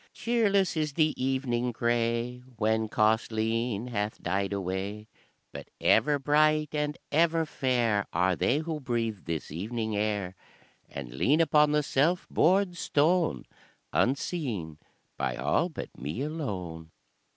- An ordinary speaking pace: No, slow, 125 wpm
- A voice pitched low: Yes, low, 120 Hz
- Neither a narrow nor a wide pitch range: No, wide, 6.7 semitones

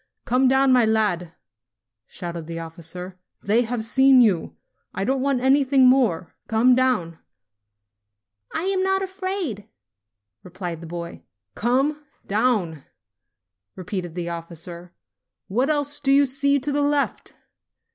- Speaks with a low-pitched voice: No, high, 240 Hz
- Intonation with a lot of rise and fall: Yes, wide, 7.6 semitones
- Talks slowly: Yes, slow, 125 wpm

